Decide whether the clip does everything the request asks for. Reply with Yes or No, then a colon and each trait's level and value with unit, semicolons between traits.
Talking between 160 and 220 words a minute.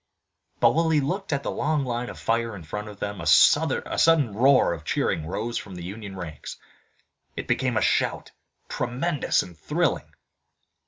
Yes: average, 170 wpm